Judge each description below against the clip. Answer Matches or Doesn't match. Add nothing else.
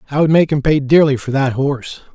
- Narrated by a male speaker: Matches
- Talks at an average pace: Doesn't match